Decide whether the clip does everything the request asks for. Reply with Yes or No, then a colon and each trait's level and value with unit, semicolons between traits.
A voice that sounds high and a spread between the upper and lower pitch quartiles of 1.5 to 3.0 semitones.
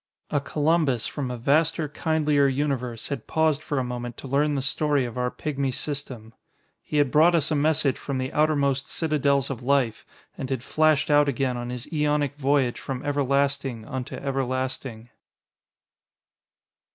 No: medium, 140 Hz; narrow, 2.6 semitones